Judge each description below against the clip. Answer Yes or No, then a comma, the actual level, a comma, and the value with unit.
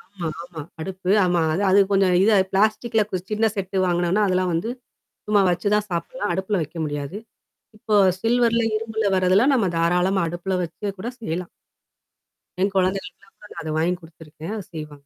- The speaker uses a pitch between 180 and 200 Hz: Yes, medium, 185 Hz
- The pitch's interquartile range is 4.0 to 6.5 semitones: No, average, 3.3 semitones